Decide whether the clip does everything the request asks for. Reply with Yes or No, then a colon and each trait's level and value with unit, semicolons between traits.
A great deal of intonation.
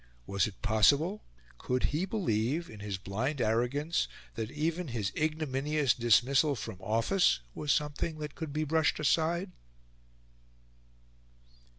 Yes: wide, 5.9 semitones